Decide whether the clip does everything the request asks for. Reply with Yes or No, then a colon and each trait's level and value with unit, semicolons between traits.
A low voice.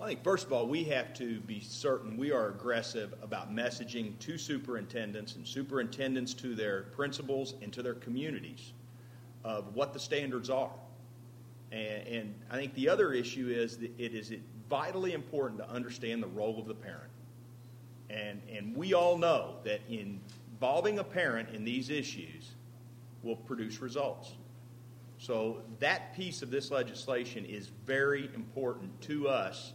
Yes: low, 120 Hz